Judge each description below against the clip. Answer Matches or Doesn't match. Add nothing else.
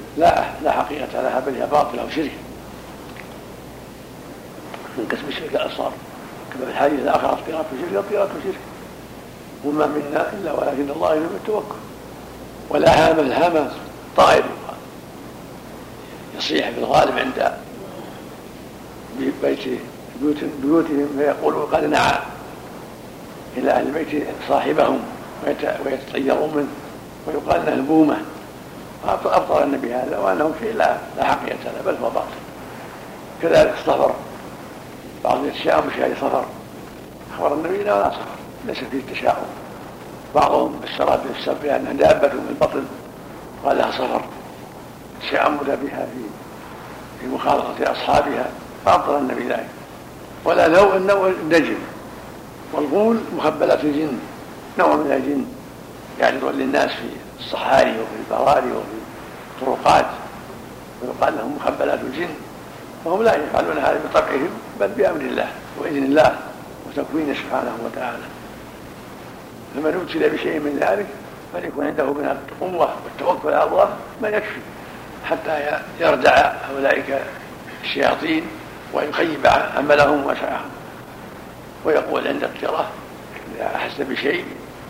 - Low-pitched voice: Doesn't match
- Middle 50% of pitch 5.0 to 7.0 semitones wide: Matches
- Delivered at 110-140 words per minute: Matches